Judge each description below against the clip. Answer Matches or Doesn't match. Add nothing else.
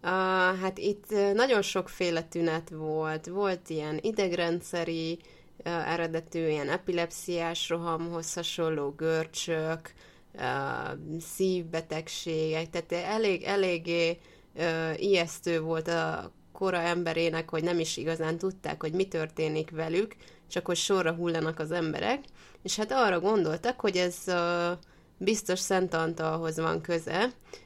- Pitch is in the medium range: Matches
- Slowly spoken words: Doesn't match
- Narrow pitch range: Matches